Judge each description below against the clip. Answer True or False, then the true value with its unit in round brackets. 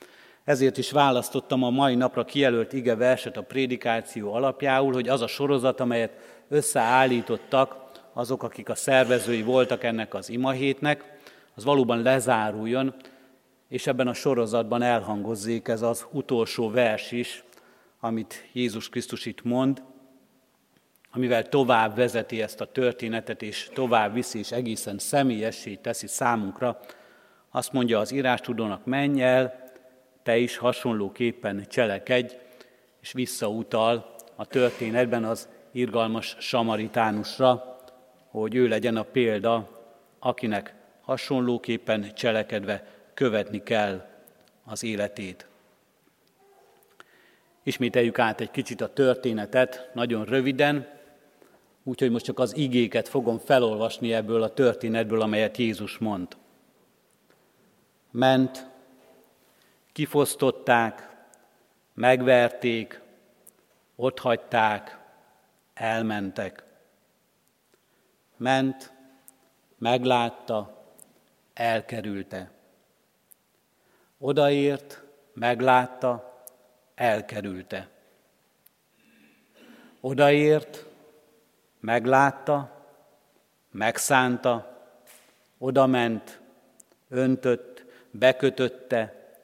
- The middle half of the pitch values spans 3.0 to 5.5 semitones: False (2.6 semitones)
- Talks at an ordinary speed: False (85 wpm)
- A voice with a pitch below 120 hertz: False (125 Hz)